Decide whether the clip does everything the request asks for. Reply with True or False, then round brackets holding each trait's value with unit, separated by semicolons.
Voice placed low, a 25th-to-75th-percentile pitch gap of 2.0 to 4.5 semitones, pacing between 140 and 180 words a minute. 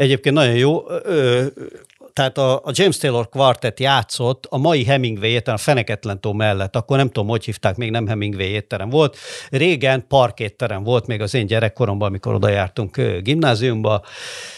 True (120 Hz; 4.0 semitones; 150 wpm)